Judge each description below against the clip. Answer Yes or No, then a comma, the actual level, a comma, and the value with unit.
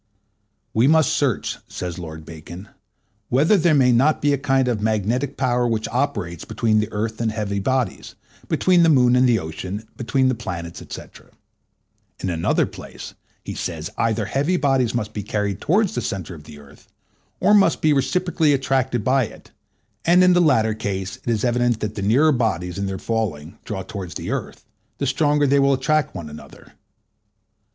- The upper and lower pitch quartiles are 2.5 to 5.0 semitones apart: No, wide, 5.6 semitones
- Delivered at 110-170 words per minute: No, average, 180 wpm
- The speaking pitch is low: Yes, low, 115 Hz